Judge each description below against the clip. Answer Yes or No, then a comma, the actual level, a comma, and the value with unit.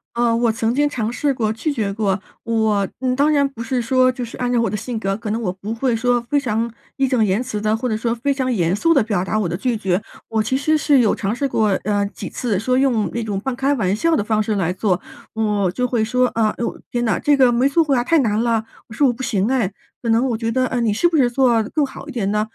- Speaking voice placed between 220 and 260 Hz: Yes, high, 230 Hz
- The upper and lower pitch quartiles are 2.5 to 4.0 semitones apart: Yes, average, 3.2 semitones